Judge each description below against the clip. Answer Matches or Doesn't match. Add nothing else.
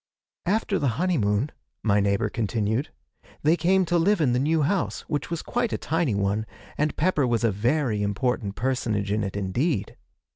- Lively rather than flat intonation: Matches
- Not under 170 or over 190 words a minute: Matches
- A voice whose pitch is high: Doesn't match